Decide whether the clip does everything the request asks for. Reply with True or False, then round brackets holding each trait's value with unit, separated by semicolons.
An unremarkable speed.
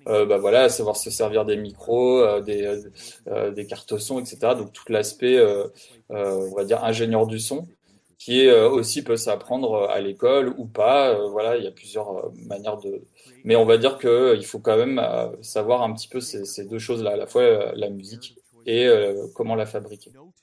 True (205 wpm)